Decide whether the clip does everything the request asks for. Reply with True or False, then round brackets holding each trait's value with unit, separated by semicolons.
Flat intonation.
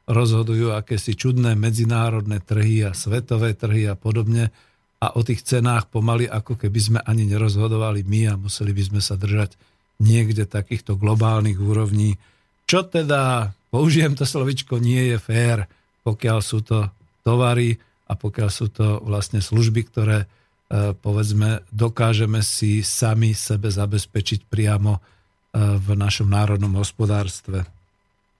True (2.0 semitones)